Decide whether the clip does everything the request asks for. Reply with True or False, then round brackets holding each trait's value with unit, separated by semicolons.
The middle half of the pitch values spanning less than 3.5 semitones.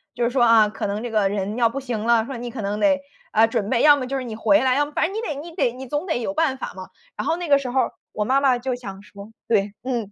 False (4.1 semitones)